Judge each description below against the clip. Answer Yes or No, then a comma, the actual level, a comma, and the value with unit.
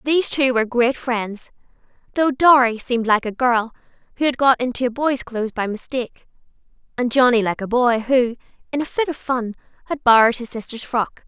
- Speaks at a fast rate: No, average, 185 wpm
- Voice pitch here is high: Yes, high, 245 Hz